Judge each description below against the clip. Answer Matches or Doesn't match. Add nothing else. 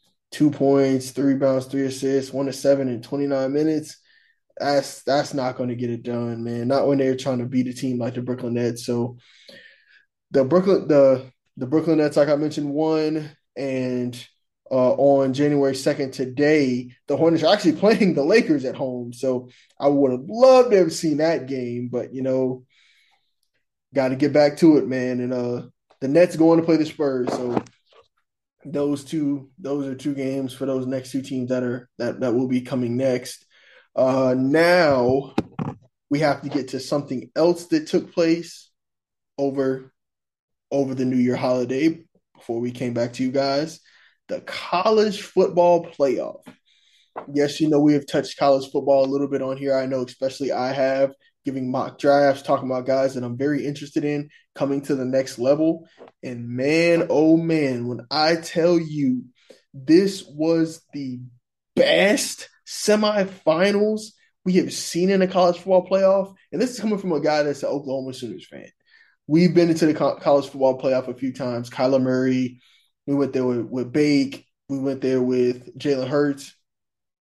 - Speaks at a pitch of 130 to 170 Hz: Matches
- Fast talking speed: Doesn't match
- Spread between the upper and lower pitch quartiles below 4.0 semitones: Matches